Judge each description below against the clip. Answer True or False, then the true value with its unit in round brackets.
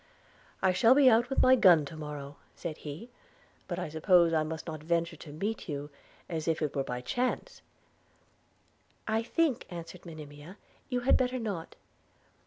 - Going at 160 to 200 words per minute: True (170 wpm)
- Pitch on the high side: False (170 Hz)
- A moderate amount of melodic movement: False (6.7 semitones)